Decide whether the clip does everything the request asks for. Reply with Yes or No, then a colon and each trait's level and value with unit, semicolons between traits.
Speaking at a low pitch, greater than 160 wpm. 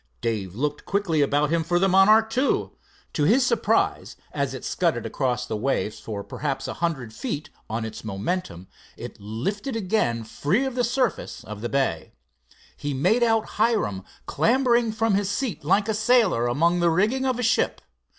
No: medium, 175 Hz; average, 175 wpm